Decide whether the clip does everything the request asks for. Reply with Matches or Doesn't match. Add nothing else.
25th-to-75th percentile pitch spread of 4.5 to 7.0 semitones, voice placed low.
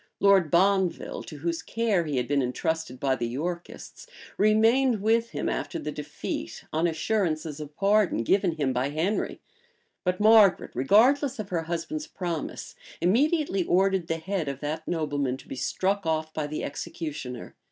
Doesn't match